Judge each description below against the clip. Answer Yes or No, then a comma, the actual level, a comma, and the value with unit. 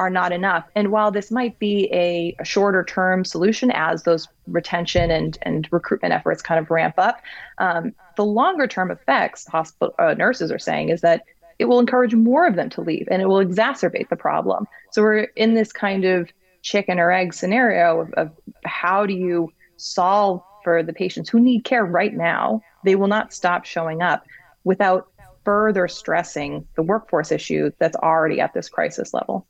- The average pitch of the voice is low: No, medium, 185 Hz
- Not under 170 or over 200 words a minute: Yes, average, 185 wpm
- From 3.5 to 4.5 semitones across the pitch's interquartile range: Yes, average, 3.9 semitones